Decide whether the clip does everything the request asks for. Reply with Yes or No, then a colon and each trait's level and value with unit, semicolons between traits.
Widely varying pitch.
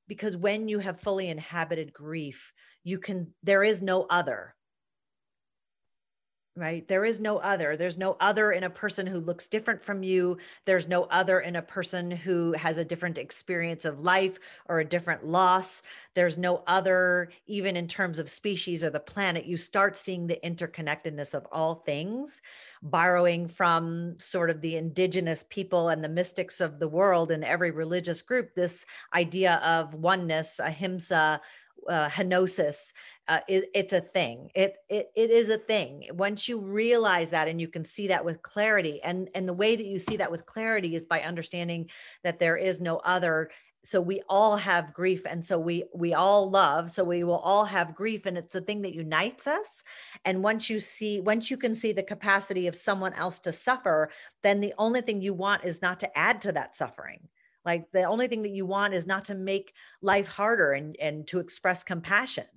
No: average, 2.8 semitones